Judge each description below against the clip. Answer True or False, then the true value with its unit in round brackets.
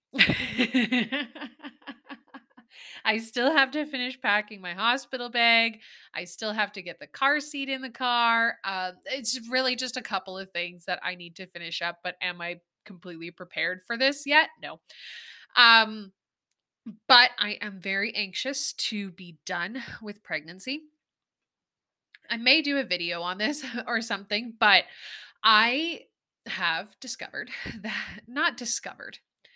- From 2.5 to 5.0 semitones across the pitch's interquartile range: False (5.4 semitones)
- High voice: True (230 Hz)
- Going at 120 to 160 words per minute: True (140 wpm)